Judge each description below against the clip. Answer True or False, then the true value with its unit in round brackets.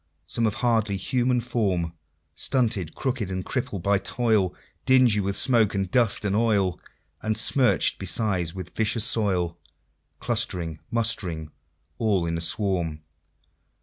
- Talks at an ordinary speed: False (130 wpm)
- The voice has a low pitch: True (100 Hz)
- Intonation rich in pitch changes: False (4.3 semitones)